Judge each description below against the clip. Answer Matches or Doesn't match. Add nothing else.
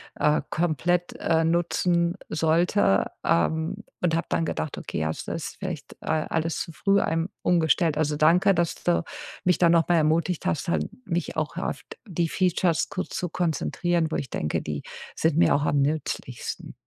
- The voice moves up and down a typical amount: Doesn't match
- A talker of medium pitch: Matches